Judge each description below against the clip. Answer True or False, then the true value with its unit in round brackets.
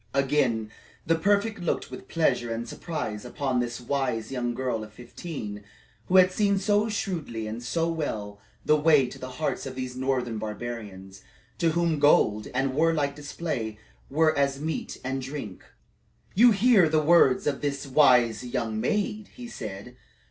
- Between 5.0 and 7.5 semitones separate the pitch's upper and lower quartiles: True (5.5 semitones)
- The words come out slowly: False (160 wpm)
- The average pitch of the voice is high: False (135 Hz)